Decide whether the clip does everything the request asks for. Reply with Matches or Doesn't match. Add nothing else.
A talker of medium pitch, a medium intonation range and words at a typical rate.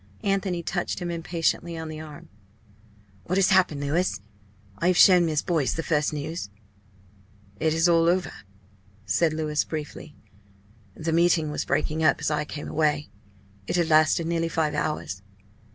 Doesn't match